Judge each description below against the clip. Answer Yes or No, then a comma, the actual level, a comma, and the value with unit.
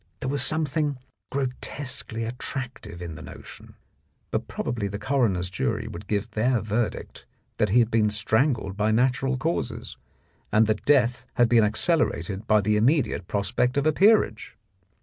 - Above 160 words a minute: No, average, 155 wpm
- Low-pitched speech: Yes, low, 115 Hz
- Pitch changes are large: No, average, 4.0 semitones